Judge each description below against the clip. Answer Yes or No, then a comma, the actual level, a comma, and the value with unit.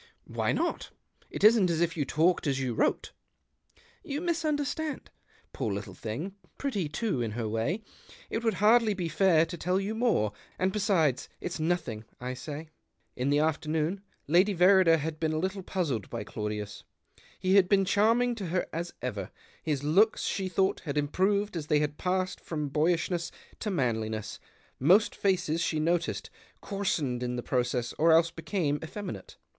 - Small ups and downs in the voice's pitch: No, wide, 5.5 semitones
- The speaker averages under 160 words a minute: No, average, 170 wpm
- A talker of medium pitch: Yes, medium, 165 Hz